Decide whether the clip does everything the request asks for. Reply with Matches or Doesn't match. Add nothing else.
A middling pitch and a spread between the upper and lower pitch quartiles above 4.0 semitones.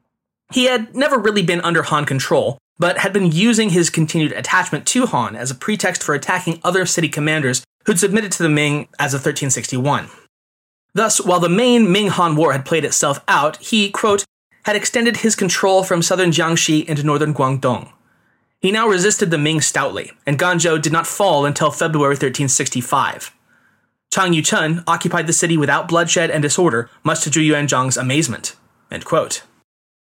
Matches